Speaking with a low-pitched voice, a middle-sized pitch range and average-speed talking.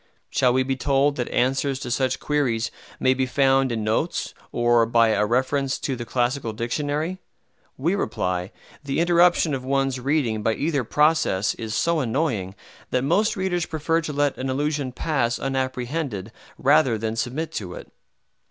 Yes: low, 130 Hz; average, 3.9 semitones; average, 160 wpm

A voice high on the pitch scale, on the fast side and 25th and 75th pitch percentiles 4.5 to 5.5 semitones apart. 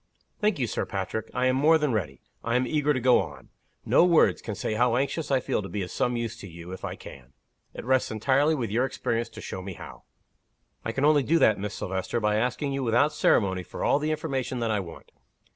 No: low, 120 Hz; fast, 240 wpm; average, 5.0 semitones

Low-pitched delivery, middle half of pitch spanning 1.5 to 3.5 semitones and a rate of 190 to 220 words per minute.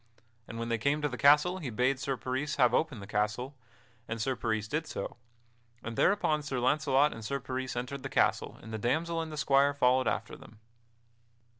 No: low, 130 Hz; average, 3.9 semitones; average, 200 wpm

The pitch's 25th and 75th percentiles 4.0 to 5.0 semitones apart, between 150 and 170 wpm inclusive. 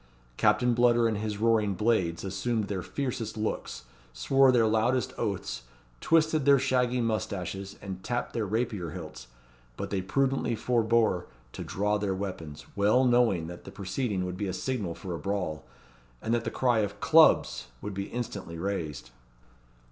Yes: average, 4.3 semitones; average, 160 wpm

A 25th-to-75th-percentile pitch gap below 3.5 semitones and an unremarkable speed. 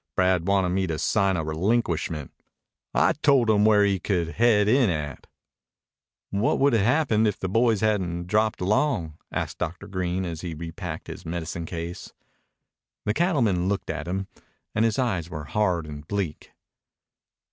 No: average, 4.3 semitones; average, 160 wpm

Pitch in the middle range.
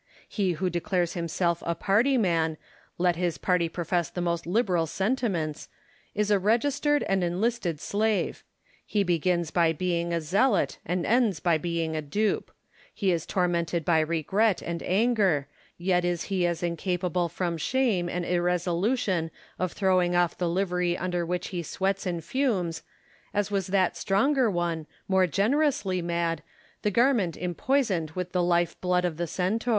Yes: medium, 180 Hz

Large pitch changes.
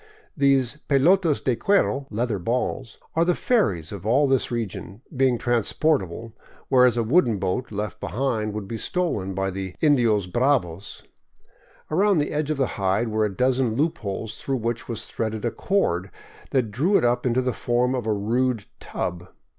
No: average, 4.5 semitones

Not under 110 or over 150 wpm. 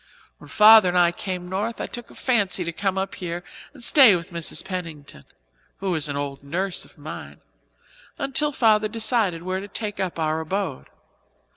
No: average, 175 wpm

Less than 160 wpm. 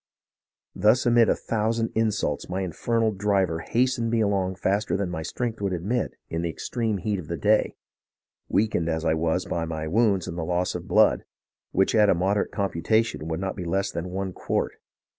No: average, 195 wpm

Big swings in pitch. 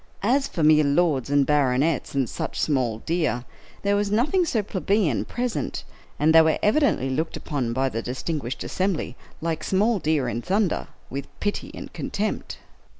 Yes: wide, 7.1 semitones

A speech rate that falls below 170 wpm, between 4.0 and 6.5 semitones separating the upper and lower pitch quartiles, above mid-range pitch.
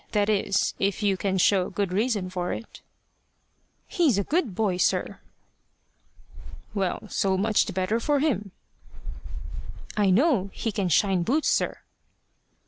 No: slow, 135 wpm; average, 3.1 semitones; high, 200 Hz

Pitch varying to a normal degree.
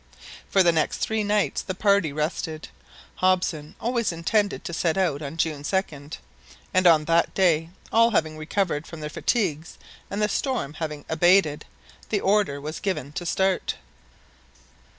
Yes: average, 4.2 semitones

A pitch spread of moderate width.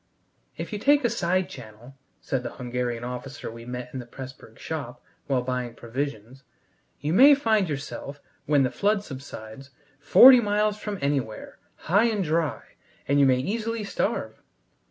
No: wide, 8.5 semitones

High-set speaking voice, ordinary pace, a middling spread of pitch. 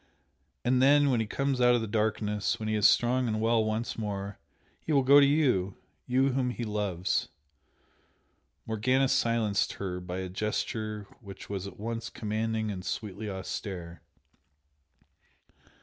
No: low, 110 Hz; average, 155 wpm; average, 3.5 semitones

